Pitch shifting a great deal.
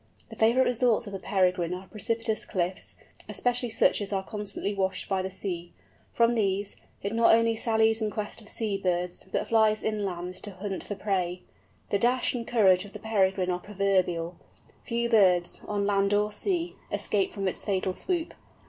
No: average, 2.9 semitones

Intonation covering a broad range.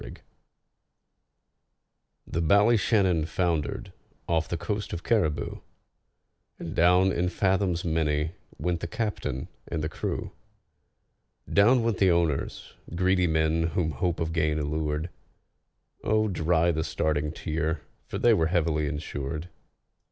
No: average, 2.9 semitones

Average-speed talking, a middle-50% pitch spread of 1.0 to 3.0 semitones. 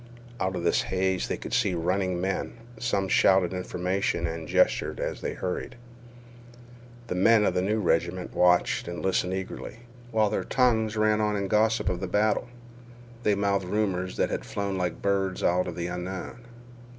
Yes: average, 175 wpm; narrow, 2.6 semitones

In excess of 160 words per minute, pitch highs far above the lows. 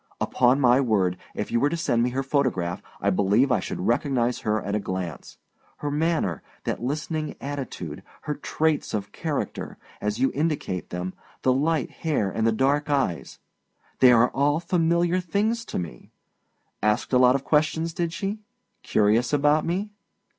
Yes: average, 170 wpm; wide, 6.2 semitones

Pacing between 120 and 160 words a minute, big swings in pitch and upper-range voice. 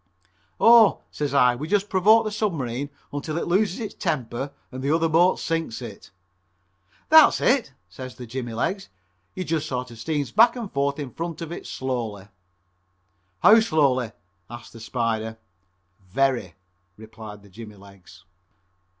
No: average, 150 wpm; wide, 6.9 semitones; medium, 140 Hz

